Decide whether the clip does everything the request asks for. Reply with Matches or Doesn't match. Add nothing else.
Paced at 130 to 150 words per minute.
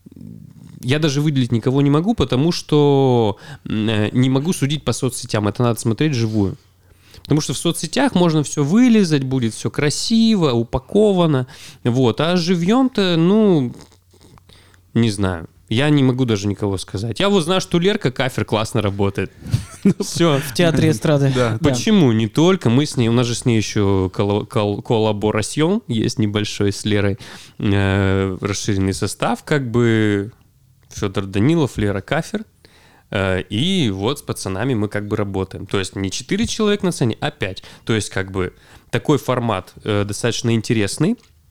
Matches